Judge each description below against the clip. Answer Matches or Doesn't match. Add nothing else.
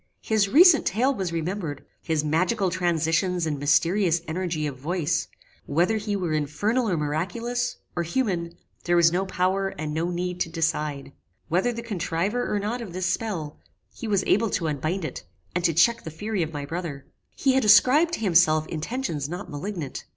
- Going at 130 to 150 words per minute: Doesn't match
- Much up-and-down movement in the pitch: Doesn't match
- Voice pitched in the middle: Matches